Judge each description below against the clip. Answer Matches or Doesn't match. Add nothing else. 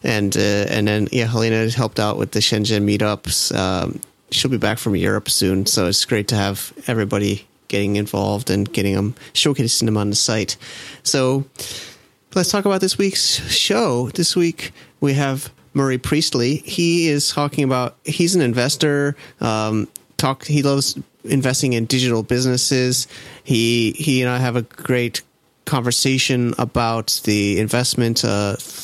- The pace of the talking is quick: Doesn't match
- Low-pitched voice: Matches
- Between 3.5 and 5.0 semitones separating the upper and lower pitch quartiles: Matches